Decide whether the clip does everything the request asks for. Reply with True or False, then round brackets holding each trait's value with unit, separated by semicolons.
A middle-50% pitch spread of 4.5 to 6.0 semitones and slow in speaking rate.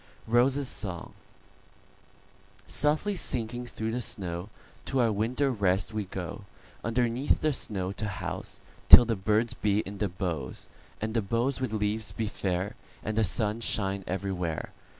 False (3.6 semitones; 125 wpm)